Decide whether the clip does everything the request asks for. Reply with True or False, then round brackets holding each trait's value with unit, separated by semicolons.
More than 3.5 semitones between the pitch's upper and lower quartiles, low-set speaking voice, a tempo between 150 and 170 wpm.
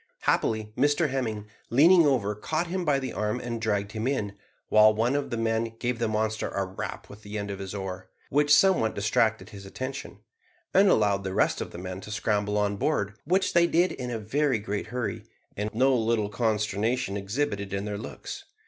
False (4.3 semitones; 110 Hz; 200 wpm)